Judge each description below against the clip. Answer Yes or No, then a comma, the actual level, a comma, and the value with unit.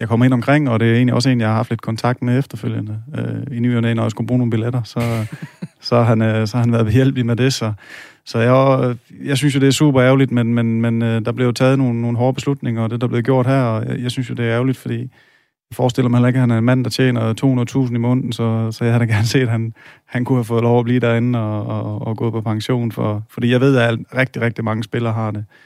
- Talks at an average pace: No, fast, 280 wpm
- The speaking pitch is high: No, low, 120 Hz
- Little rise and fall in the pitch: Yes, narrow, 2.0 semitones